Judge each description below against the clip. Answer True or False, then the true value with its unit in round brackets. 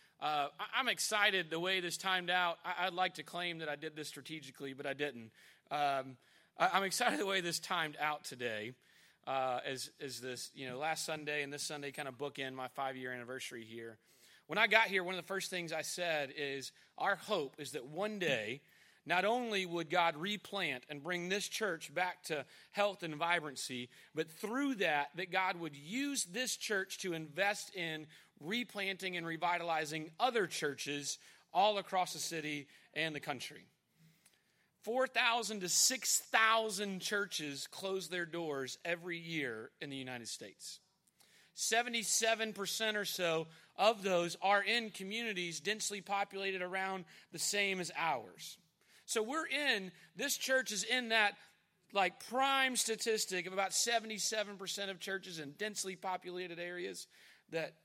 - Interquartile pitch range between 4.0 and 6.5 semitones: True (5.0 semitones)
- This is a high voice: False (180 Hz)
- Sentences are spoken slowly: False (160 wpm)